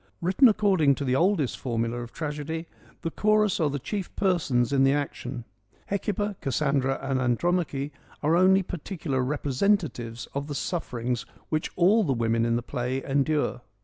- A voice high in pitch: No, medium, 145 Hz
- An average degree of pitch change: No, wide, 5.8 semitones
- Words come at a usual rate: Yes, average, 155 wpm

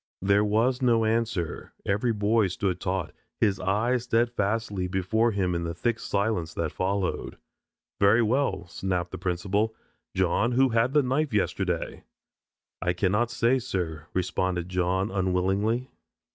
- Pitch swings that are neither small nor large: Yes, average, 3.9 semitones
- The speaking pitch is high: No, low, 100 Hz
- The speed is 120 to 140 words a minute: Yes, slow, 135 wpm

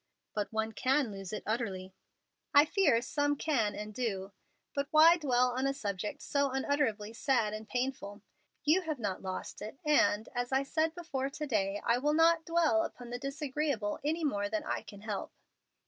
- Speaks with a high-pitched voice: Yes, very high, 255 Hz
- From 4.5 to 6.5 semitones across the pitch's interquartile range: Yes, wide, 5.6 semitones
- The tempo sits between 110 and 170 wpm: No, average, 180 wpm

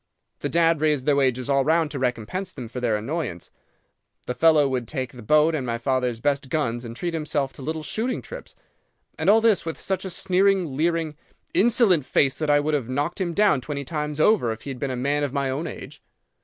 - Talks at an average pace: No, fast, 225 wpm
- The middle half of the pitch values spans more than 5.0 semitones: No, average, 4.3 semitones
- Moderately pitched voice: Yes, medium, 145 Hz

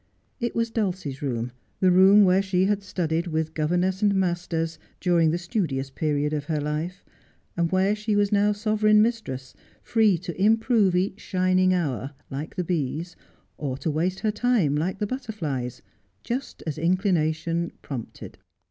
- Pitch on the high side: No, medium, 180 Hz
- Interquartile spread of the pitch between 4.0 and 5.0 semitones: Yes, average, 4.6 semitones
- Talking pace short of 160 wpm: No, average, 165 wpm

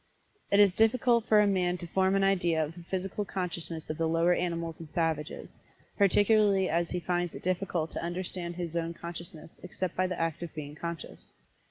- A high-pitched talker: No, medium, 175 Hz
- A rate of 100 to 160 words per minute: No, average, 195 wpm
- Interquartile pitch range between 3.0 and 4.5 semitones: No, narrow, 2.4 semitones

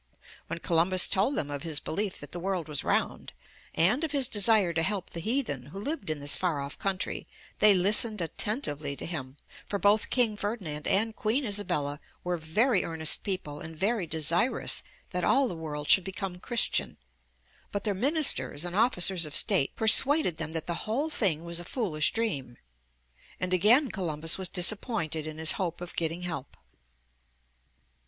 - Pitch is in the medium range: Yes, medium, 180 Hz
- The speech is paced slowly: No, average, 175 wpm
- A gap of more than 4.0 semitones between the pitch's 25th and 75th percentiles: Yes, average, 5.2 semitones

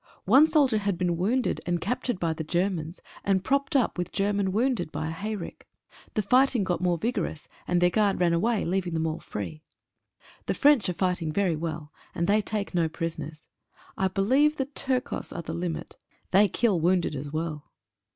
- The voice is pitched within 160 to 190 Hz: Yes, medium, 185 Hz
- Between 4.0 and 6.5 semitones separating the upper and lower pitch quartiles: Yes, average, 4.5 semitones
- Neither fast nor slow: Yes, average, 190 wpm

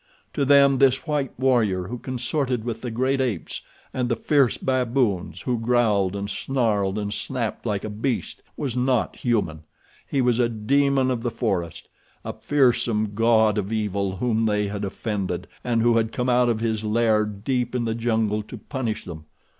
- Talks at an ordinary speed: Yes, average, 175 wpm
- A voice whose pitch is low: Yes, low, 115 Hz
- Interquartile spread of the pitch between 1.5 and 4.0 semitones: Yes, average, 3.2 semitones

